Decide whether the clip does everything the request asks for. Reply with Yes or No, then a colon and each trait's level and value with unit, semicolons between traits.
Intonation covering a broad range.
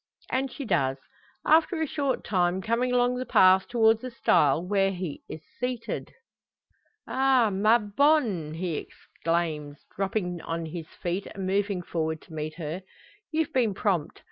Yes: wide, 6.7 semitones